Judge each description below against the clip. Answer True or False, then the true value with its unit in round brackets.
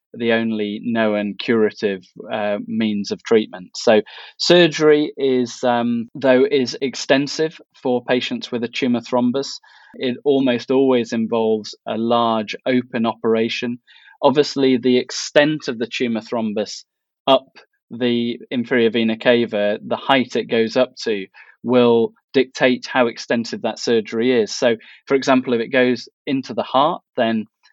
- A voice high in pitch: False (120 Hz)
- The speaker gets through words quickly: False (140 wpm)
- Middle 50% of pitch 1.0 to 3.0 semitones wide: True (2.4 semitones)